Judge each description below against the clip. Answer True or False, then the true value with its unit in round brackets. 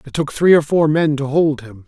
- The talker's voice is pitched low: False (150 Hz)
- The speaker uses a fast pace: True (290 wpm)